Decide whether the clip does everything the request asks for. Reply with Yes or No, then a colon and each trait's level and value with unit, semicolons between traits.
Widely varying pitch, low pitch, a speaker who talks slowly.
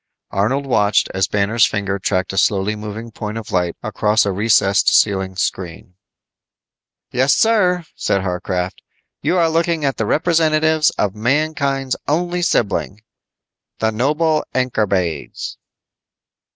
Yes: wide, 7.6 semitones; low, 110 Hz; slow, 125 wpm